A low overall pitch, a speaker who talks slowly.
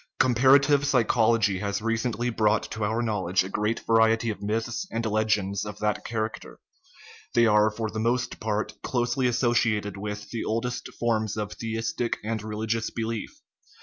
No: low, 110 Hz; average, 150 wpm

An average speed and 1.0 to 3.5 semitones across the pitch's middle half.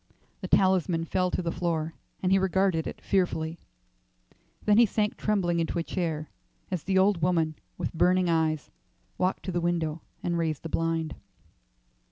Yes: average, 165 wpm; narrow, 2.4 semitones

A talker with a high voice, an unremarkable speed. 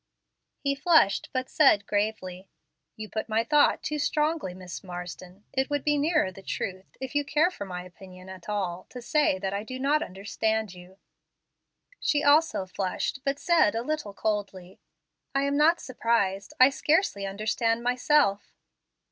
Yes: high, 220 Hz; average, 160 wpm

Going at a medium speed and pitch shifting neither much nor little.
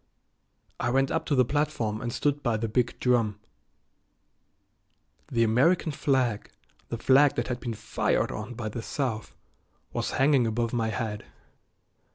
Yes: average, 150 wpm; average, 3.3 semitones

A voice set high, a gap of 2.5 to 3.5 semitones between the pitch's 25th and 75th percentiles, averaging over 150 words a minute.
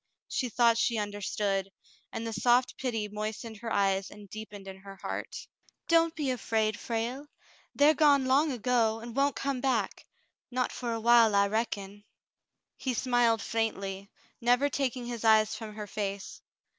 Yes: high, 225 Hz; average, 3.1 semitones; average, 160 wpm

